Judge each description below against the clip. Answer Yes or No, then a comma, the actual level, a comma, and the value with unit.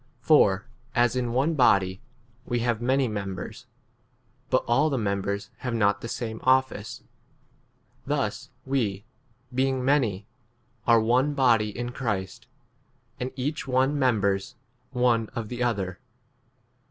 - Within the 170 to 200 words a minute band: No, slow, 135 wpm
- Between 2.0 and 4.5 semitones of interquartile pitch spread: Yes, average, 4.0 semitones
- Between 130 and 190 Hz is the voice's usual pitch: No, low, 120 Hz